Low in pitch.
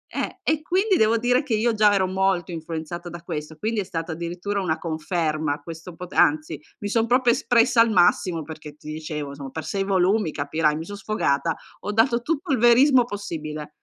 No: medium, 180 Hz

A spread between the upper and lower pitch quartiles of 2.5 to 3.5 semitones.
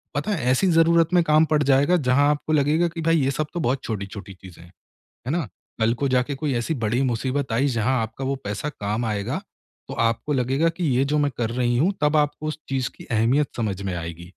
No: average, 5.0 semitones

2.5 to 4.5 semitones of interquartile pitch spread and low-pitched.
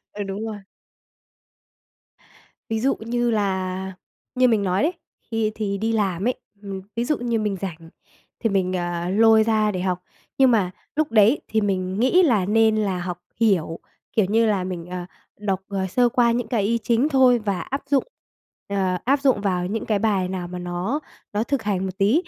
No: average, 3.6 semitones; high, 210 Hz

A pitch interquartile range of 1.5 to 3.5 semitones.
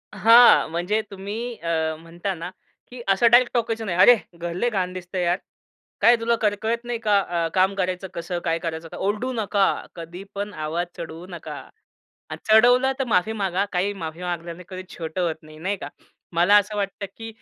No: average, 4.2 semitones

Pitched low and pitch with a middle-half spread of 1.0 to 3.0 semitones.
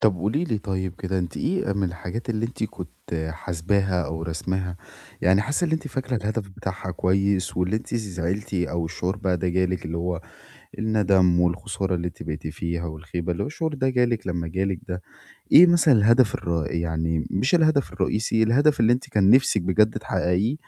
No: very low, 95 Hz; average, 4.2 semitones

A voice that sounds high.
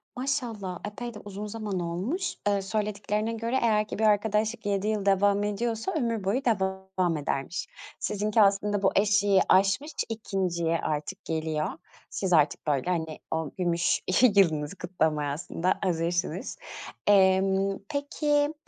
Yes: high, 195 Hz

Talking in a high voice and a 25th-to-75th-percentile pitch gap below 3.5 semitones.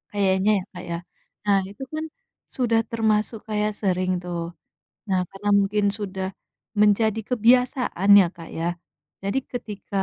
Yes: high, 205 Hz; average, 2.8 semitones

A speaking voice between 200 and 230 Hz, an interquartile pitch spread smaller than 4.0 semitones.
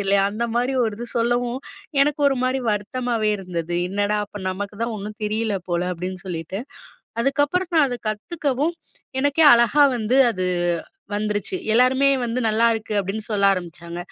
No: high, 220 Hz; average, 4.3 semitones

